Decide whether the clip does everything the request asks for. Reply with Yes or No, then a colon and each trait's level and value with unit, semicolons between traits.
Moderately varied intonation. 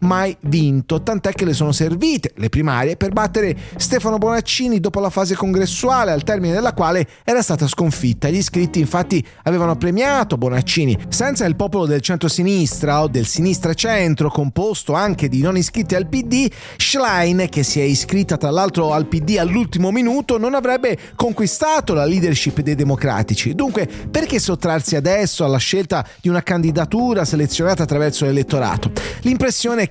No: wide, 5.9 semitones